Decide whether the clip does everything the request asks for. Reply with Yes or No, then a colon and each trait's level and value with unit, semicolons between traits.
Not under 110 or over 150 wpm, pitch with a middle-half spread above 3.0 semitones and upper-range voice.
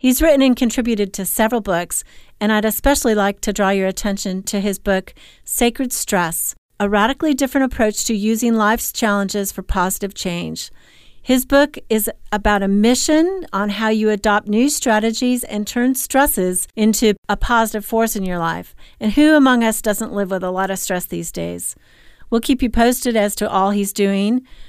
No: average, 180 wpm; average, 3.5 semitones; high, 215 Hz